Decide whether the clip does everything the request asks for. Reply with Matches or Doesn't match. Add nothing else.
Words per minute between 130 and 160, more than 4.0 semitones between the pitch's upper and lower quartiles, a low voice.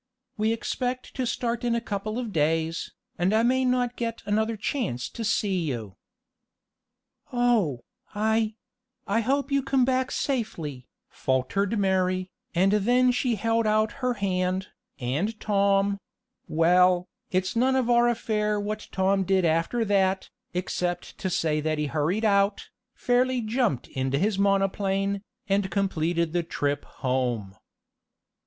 Doesn't match